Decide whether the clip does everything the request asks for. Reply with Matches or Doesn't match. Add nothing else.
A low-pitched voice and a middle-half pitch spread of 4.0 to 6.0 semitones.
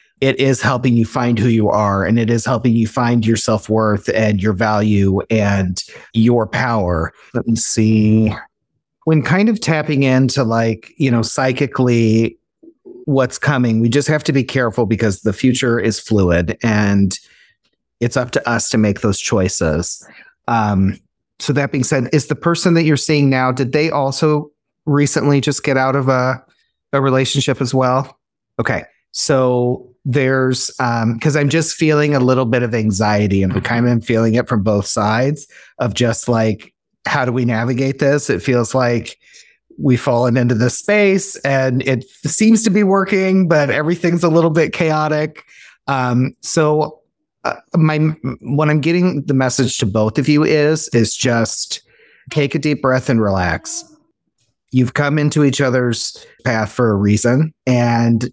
Matches